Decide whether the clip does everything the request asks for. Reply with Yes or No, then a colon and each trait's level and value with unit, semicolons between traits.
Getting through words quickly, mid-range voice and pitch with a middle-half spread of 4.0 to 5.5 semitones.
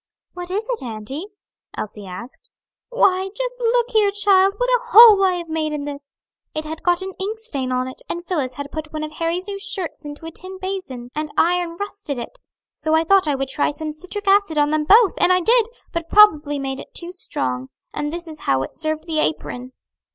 No: fast, 215 wpm; very high, 330 Hz; average, 5.1 semitones